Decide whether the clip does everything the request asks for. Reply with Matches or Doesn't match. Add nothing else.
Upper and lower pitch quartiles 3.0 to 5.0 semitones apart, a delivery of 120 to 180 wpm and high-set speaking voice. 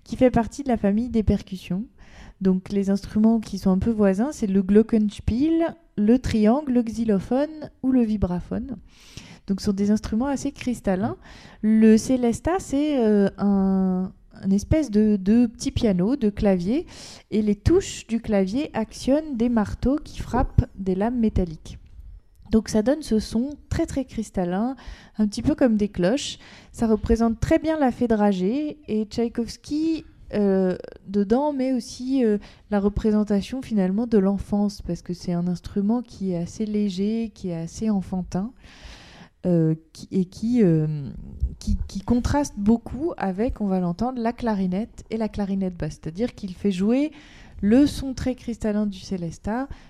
Matches